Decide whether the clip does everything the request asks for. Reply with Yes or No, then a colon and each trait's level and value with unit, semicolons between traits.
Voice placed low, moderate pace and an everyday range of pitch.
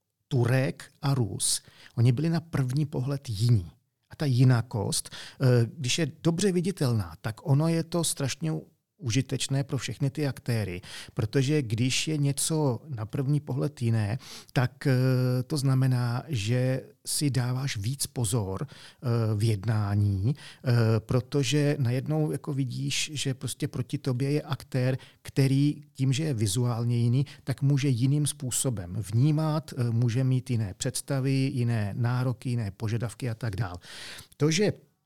Yes: low, 130 Hz; average, 135 wpm; average, 3.0 semitones